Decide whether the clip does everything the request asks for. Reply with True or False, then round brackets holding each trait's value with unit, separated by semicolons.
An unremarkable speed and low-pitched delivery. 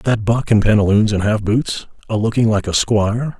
True (195 wpm; 110 Hz)